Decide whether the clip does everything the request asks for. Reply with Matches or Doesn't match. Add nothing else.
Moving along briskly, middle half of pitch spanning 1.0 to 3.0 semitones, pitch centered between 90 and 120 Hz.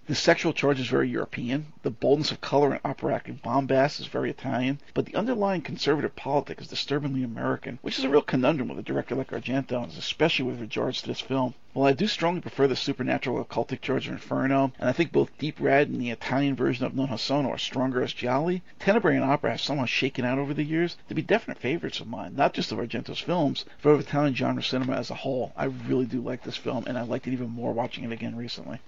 Doesn't match